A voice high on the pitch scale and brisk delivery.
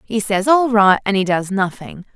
Yes: high, 205 Hz; fast, 220 wpm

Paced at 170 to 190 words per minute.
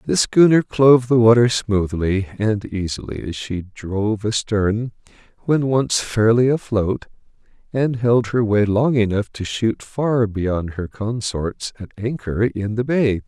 No: average, 150 wpm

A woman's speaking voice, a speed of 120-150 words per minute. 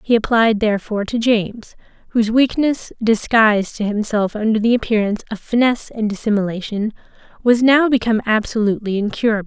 Yes: female; average, 140 wpm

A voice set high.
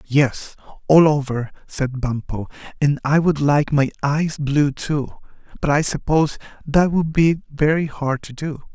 No: medium, 145 Hz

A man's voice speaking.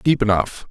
Yes: male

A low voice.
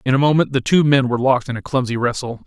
Yes: low, 130 Hz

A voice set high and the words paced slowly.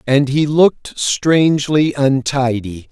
No: medium, 140 Hz; slow, 105 wpm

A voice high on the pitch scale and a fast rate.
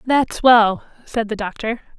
No: high, 225 Hz; average, 150 wpm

